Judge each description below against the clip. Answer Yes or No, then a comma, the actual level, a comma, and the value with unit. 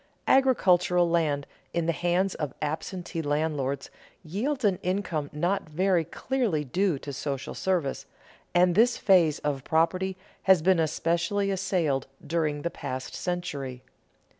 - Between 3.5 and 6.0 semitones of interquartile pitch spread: Yes, average, 4.2 semitones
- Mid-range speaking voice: Yes, medium, 170 Hz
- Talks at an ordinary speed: No, slow, 130 wpm